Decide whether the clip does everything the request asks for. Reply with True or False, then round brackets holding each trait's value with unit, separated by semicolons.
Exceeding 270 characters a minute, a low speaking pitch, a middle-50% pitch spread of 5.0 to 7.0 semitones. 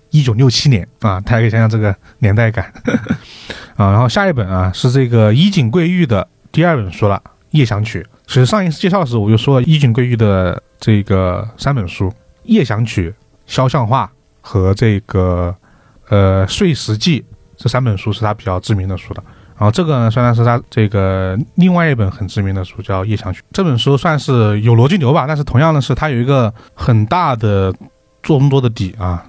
True (290 characters per minute; 115 Hz; 5.5 semitones)